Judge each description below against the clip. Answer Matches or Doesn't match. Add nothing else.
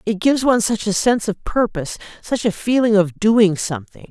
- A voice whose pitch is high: Matches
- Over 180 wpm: Matches